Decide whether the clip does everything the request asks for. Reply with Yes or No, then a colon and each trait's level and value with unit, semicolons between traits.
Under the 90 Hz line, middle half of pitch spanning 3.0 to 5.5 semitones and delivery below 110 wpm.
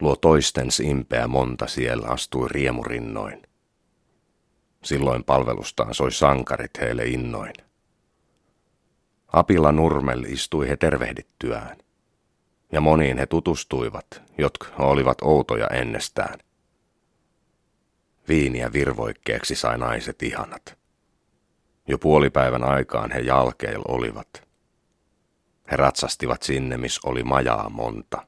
No: very low, 65 Hz; narrow, 2.4 semitones; slow, 95 wpm